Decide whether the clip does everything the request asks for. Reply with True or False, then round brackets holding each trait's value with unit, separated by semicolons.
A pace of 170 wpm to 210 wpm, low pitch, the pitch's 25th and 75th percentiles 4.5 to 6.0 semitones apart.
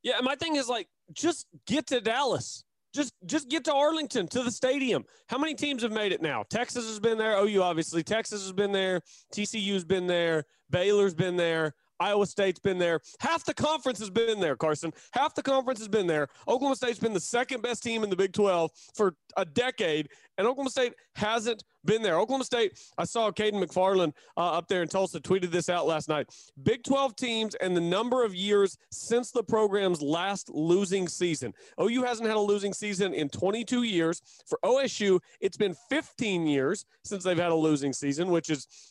False (200 wpm; 205 Hz; 5.5 semitones)